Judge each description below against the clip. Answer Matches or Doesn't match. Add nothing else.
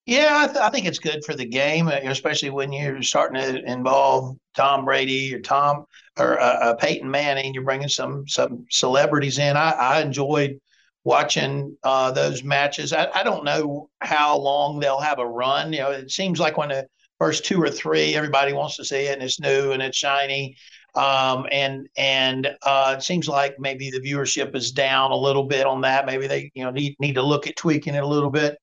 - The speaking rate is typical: Doesn't match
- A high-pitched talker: Doesn't match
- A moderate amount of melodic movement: Doesn't match